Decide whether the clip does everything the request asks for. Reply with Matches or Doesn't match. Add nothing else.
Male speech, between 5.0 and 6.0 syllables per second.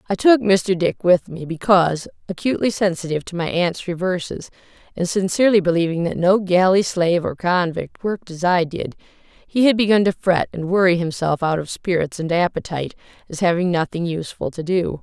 Doesn't match